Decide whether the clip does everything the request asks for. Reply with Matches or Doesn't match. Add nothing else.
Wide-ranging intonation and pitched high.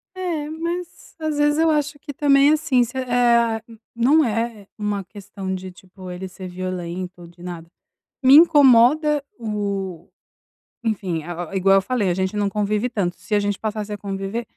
Matches